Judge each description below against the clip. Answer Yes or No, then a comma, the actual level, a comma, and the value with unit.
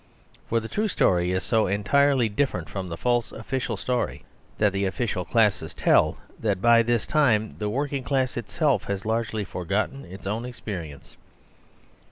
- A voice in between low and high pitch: No, low, 110 Hz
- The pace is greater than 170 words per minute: No, average, 160 wpm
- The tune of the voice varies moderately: Yes, average, 4.3 semitones